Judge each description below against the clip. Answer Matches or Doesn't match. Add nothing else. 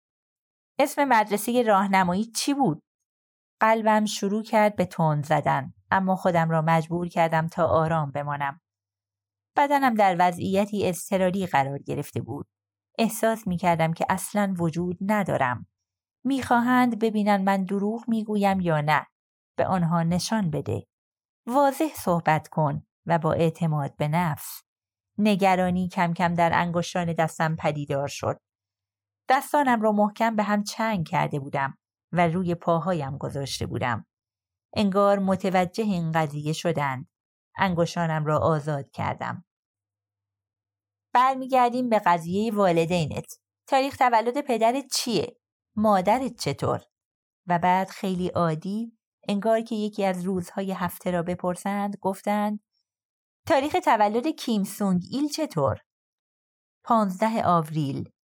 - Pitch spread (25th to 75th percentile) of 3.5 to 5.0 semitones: Doesn't match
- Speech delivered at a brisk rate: Doesn't match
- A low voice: Doesn't match